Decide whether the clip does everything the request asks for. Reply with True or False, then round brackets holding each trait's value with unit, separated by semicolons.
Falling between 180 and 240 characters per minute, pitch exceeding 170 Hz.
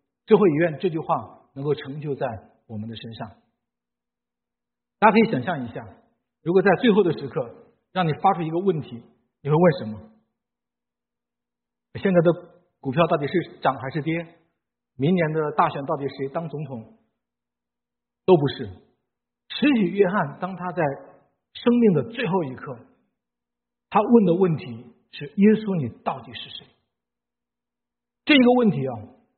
False (210 characters per minute; 140 Hz)